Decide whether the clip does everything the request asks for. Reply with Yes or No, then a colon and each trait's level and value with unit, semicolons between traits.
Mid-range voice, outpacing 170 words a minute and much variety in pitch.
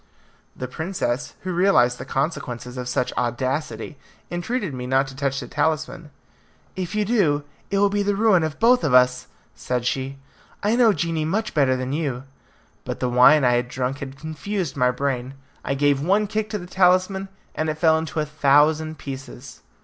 Yes: medium, 150 Hz; average, 185 wpm; wide, 5.9 semitones